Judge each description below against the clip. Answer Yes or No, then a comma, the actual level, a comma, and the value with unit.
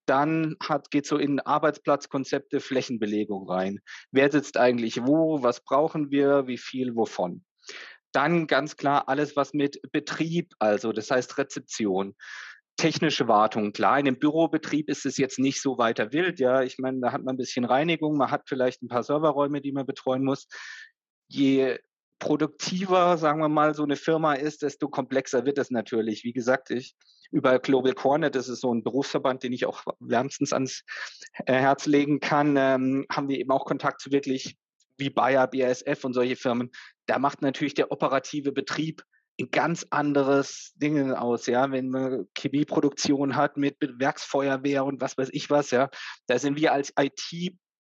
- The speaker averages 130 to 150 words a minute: No, average, 175 wpm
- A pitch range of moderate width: No, narrow, 2.3 semitones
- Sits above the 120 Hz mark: Yes, medium, 140 Hz